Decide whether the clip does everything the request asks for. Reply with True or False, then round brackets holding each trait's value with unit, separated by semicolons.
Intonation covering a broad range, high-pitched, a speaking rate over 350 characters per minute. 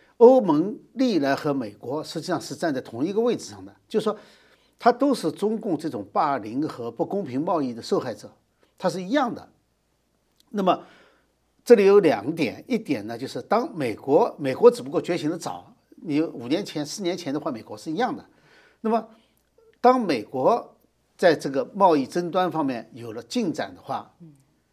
False (6.7 semitones; 215 Hz; 255 characters per minute)